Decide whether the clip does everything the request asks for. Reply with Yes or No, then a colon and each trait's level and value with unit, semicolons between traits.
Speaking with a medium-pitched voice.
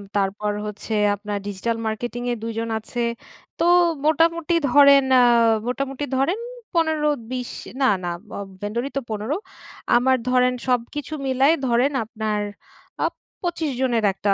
No: very high, 250 Hz